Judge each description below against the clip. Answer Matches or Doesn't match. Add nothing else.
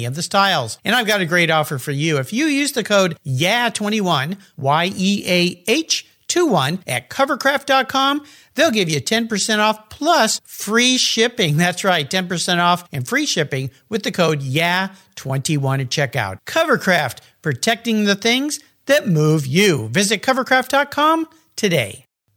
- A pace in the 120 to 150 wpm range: Matches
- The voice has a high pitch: Matches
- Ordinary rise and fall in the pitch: Doesn't match